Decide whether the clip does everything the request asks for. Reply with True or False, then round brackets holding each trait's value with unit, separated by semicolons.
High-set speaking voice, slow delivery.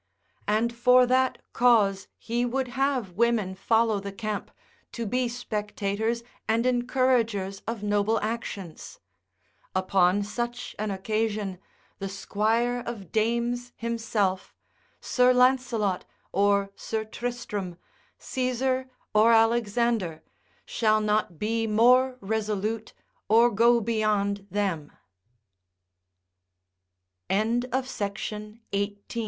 True (225 Hz; 85 wpm)